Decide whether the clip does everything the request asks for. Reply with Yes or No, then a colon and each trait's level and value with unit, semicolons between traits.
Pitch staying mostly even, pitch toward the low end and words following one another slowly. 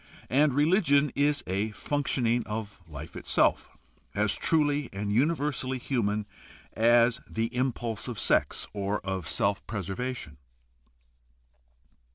No: wide, 5.5 semitones; low, 120 Hz; slow, 115 wpm